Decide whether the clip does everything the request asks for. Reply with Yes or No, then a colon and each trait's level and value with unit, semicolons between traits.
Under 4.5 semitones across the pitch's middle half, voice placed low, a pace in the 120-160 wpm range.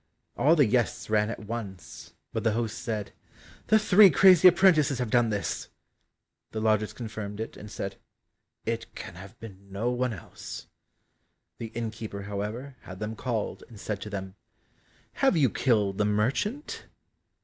Yes: average, 3.4 semitones; low, 110 Hz; average, 155 wpm